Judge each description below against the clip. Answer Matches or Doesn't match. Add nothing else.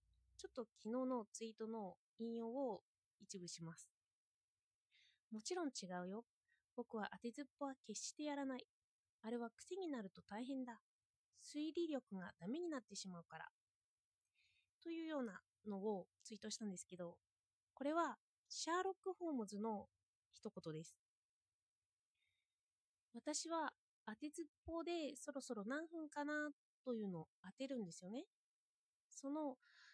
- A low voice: Doesn't match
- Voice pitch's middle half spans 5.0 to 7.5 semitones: Doesn't match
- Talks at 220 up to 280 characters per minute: Matches